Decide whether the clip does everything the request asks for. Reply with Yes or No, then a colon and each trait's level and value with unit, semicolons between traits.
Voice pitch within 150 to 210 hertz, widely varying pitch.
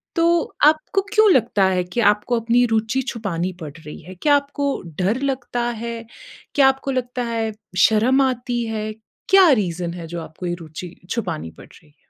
No: high, 230 Hz; wide, 6.7 semitones